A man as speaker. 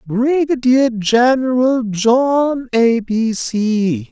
Yes: male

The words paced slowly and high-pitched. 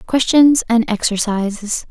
Yes: slow, 95 wpm; high, 235 Hz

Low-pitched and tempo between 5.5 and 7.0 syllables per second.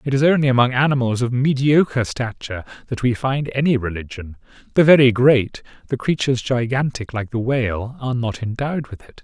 Yes: low, 125 Hz; 5.7 syllables/s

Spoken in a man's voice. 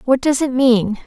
No: female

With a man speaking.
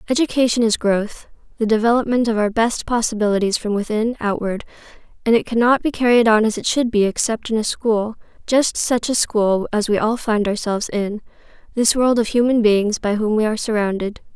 No: female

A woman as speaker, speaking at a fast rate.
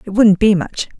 Yes: female; fast, 240 wpm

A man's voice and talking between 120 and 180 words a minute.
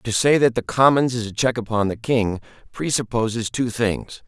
No: male; average, 195 wpm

